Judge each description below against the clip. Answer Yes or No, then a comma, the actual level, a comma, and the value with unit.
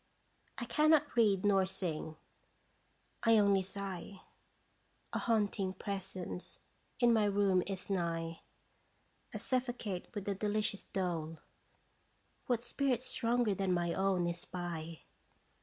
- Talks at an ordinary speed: No, slow, 115 wpm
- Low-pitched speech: No, high, 195 Hz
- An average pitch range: Yes, average, 3.8 semitones